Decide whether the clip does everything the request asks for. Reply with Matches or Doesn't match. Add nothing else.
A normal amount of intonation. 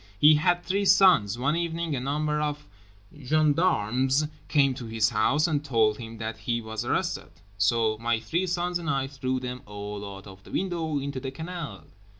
Doesn't match